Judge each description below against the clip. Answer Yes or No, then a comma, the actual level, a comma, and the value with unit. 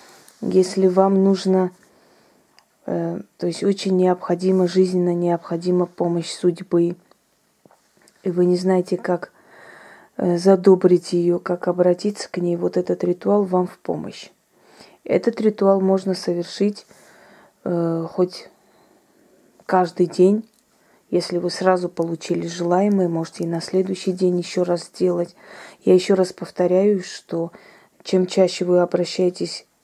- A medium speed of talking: Yes, average, 120 wpm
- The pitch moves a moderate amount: No, narrow, 1.3 semitones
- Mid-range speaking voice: Yes, medium, 180 Hz